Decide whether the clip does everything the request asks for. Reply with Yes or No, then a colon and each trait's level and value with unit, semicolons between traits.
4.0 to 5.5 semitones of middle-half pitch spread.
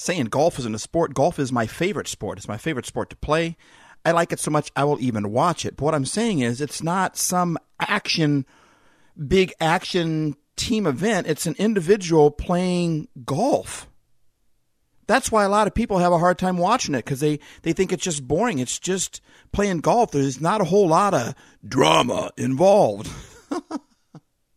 Yes: average, 4.7 semitones